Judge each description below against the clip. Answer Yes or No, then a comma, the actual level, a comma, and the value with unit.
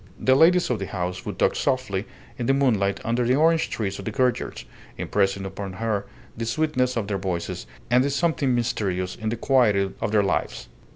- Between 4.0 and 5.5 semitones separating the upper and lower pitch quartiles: Yes, average, 4.9 semitones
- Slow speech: No, average, 195 wpm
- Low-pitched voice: Yes, low, 115 Hz